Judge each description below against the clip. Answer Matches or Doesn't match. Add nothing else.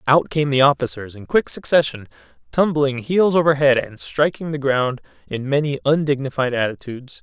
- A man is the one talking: Matches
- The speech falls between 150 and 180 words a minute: Matches